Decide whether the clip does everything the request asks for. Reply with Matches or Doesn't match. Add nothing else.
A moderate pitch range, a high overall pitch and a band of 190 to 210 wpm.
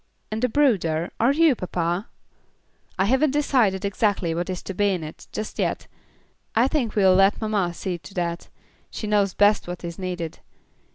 Doesn't match